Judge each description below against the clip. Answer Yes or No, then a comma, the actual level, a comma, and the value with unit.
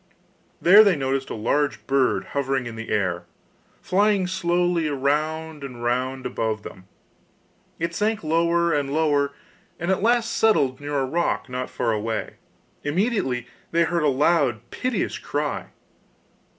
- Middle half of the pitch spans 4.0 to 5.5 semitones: Yes, average, 4.9 semitones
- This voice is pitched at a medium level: Yes, medium, 145 Hz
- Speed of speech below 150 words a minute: Yes, average, 140 wpm